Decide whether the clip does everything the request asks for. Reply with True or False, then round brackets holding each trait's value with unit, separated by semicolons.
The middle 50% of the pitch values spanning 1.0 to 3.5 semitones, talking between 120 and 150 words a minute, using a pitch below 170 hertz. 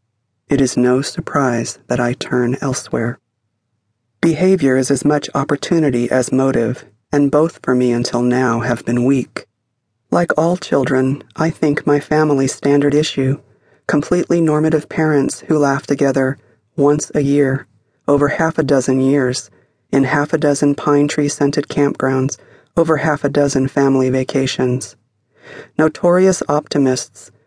True (2.8 semitones; 140 wpm; 140 Hz)